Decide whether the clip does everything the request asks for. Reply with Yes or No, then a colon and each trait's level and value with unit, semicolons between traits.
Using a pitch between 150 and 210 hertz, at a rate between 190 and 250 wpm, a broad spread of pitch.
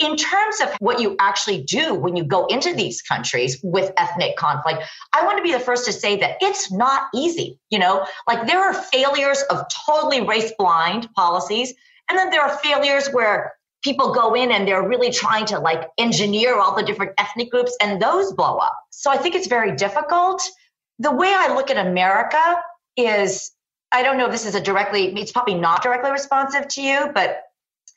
No: high, 245 Hz; average, 200 wpm; wide, 6.9 semitones